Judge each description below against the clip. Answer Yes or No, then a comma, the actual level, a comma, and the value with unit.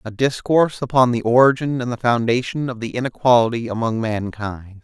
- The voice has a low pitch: Yes, low, 120 Hz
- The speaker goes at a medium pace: Yes, average, 160 wpm